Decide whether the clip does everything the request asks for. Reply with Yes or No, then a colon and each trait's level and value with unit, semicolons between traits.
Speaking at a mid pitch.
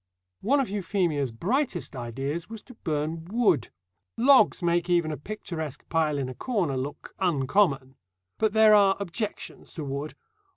Yes: medium, 170 Hz